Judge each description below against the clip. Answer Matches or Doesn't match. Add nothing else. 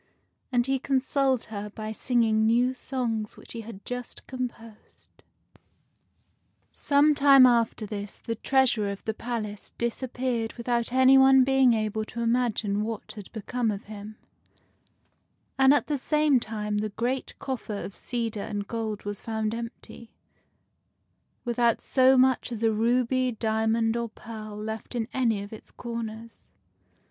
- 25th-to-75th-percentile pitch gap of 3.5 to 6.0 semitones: Doesn't match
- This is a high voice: Matches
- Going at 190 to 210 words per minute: Doesn't match